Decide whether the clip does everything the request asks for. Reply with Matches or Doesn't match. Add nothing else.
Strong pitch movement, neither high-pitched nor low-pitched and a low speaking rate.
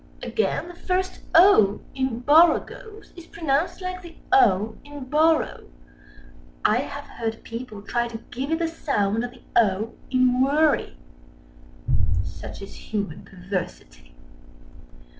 Doesn't match